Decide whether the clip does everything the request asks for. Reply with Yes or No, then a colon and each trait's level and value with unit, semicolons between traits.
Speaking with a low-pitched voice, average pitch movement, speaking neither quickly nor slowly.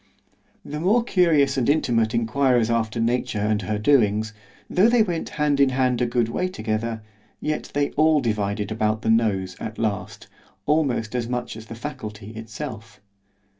Yes: low, 115 Hz; average, 4.6 semitones; average, 165 wpm